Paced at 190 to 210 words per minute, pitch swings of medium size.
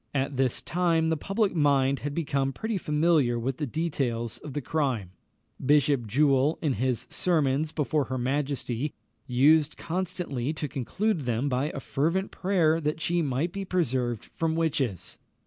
No: average, 155 wpm; average, 3.8 semitones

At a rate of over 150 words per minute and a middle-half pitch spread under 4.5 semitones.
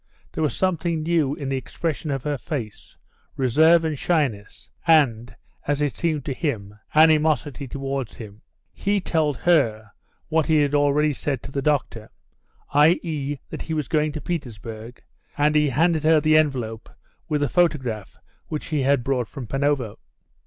Yes: average, 160 wpm; average, 3.4 semitones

